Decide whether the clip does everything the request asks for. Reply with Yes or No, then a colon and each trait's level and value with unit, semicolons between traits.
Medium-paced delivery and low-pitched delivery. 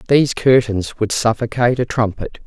Yes: average, 145 wpm; low, 115 Hz